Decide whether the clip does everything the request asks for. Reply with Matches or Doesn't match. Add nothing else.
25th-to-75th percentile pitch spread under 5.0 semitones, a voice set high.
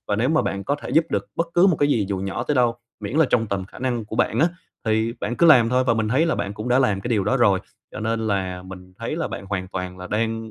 Doesn't match